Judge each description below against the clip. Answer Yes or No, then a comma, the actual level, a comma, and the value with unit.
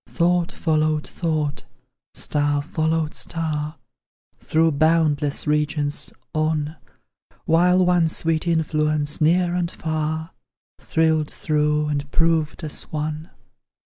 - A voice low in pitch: No, medium, 155 Hz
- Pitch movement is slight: Yes, narrow, 1.5 semitones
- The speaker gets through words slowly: Yes, slow, 100 wpm